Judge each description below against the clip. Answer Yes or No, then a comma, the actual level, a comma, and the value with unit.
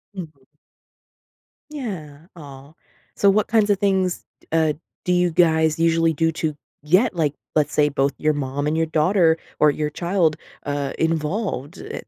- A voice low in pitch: No, medium, 160 Hz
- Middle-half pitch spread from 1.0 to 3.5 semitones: Yes, average, 3.2 semitones